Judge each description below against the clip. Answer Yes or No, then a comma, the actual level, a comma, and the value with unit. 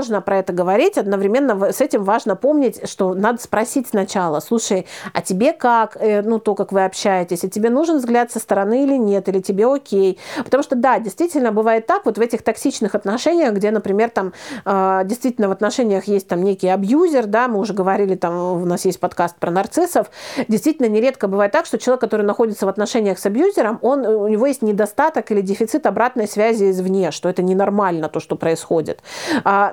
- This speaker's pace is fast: Yes, fast, 190 wpm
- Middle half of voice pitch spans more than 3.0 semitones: Yes, average, 3.9 semitones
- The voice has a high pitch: Yes, high, 210 Hz